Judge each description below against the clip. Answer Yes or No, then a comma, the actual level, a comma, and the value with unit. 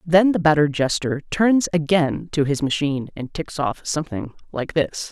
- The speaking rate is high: No, average, 175 wpm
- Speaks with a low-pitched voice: No, medium, 155 Hz